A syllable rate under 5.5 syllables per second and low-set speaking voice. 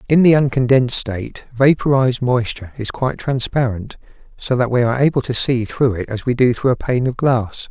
No: 5.6 syllables/s; low, 125 Hz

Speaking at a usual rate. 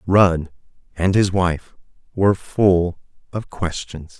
No: slow, 115 wpm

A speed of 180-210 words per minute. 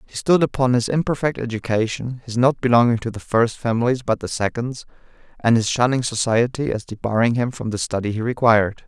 Yes: average, 190 wpm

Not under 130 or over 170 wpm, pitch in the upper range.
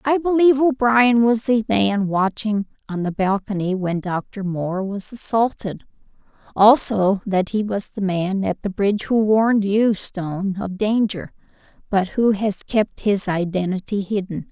Yes: average, 155 wpm; high, 205 Hz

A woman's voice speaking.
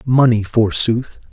No: male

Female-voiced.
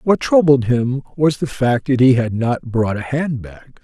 No: male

